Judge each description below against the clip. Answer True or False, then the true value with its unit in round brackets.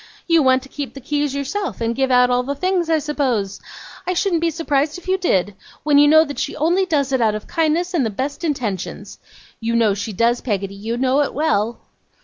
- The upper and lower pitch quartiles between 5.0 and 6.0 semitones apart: True (5.4 semitones)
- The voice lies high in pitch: True (275 Hz)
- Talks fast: True (225 wpm)